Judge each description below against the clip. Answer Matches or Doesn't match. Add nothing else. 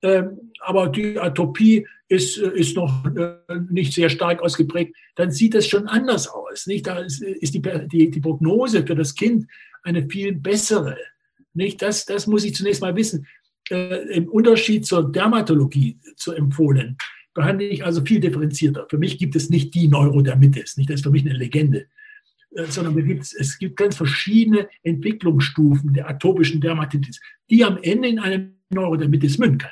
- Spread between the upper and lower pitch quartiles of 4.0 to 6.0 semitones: Matches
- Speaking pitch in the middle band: Matches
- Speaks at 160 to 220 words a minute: Matches